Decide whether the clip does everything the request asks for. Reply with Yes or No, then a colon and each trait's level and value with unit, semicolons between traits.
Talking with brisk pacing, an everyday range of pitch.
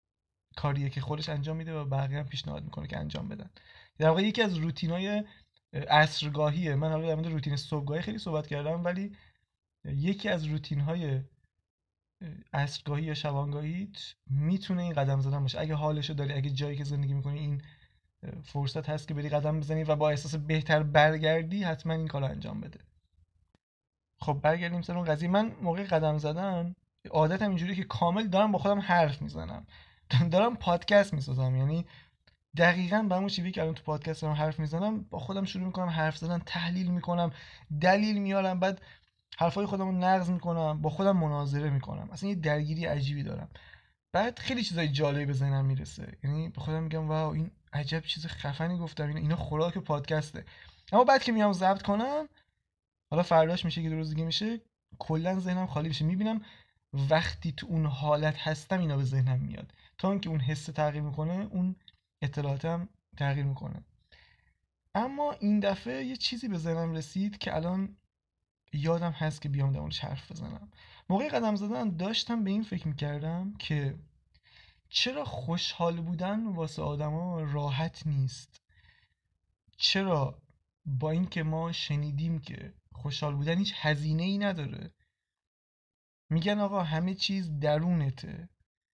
Yes: fast, 160 wpm; average, 3.9 semitones